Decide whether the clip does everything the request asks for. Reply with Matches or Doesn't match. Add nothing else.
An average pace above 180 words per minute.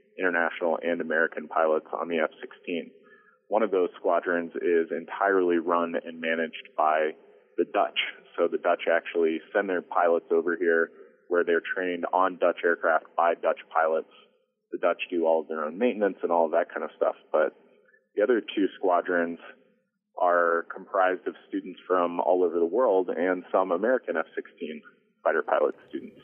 Doesn't match